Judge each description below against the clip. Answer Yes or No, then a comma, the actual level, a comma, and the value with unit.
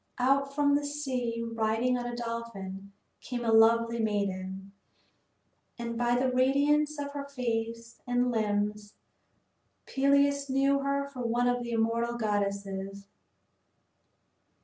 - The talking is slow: Yes, slow, 125 wpm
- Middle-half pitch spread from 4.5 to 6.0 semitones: No, average, 3.6 semitones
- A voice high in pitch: Yes, high, 235 Hz